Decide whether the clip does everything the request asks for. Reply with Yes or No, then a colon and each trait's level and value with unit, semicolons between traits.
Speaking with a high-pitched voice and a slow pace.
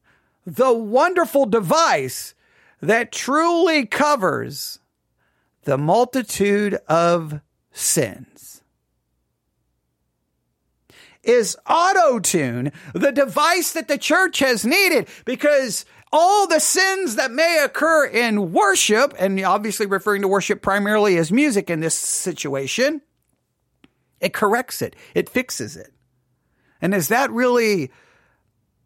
Yes: high, 230 Hz; slow, 105 wpm